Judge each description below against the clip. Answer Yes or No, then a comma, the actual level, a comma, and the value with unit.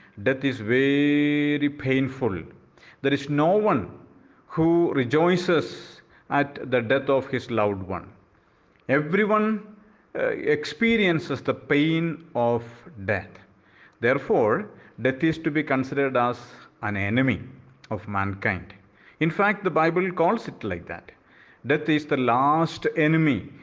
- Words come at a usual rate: No, slow, 120 wpm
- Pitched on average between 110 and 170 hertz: Yes, medium, 140 Hz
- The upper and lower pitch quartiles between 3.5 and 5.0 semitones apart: No, wide, 5.6 semitones